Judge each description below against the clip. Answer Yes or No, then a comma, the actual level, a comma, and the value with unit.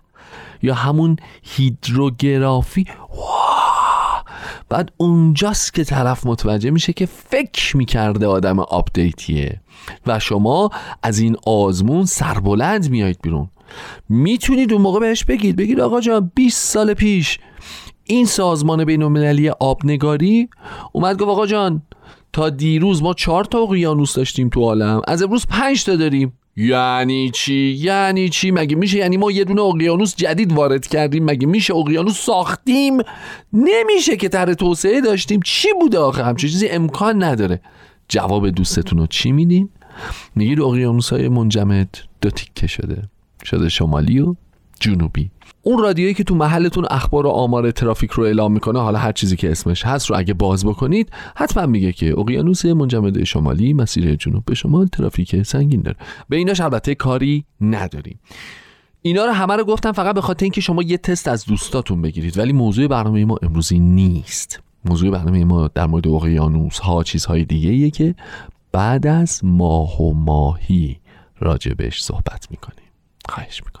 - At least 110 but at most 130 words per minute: No, average, 150 wpm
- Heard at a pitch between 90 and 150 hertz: Yes, low, 135 Hz